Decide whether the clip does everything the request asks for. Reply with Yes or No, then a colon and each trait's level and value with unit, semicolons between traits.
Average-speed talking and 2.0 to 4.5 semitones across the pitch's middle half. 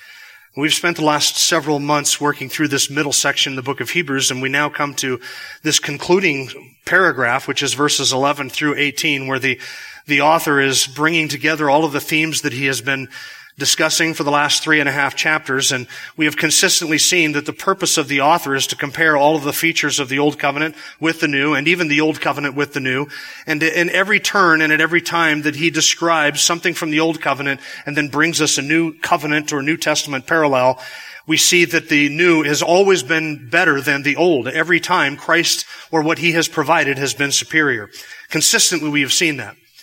No: fast, 215 wpm; narrow, 2.5 semitones